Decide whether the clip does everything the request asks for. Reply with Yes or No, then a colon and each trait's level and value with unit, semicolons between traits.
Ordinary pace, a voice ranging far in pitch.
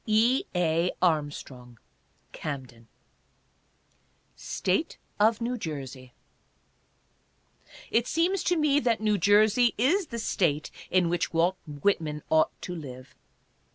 No: slow, 110 wpm; wide, 7.7 semitones